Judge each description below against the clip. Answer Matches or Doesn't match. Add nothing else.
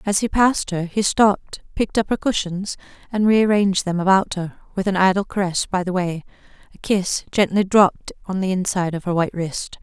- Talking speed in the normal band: Doesn't match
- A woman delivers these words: Matches